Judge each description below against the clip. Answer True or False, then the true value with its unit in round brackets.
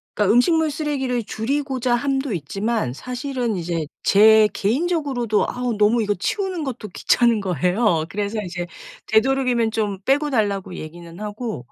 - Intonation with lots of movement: False (4.8 semitones)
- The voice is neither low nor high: False (225 Hz)